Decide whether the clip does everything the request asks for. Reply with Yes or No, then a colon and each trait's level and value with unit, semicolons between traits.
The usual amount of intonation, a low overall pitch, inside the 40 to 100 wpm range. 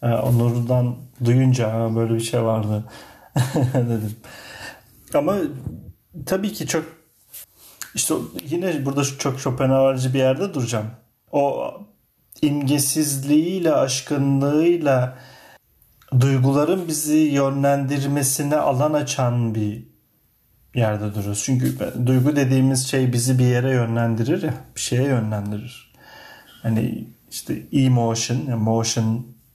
Yes: average, 3.4 semitones; low, 130 Hz; slow, 95 wpm